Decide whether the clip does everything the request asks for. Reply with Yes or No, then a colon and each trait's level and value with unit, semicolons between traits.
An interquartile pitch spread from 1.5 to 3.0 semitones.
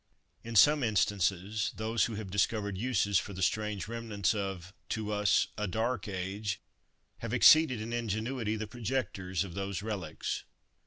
Yes: average, 2.7 semitones